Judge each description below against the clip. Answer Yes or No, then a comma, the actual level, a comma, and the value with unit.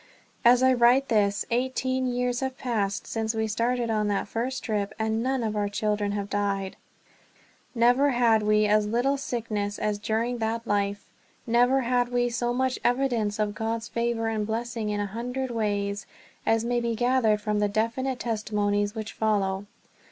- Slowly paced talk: No, average, 170 wpm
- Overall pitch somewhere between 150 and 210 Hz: No, high, 225 Hz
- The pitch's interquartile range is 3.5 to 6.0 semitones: No, average, 2.7 semitones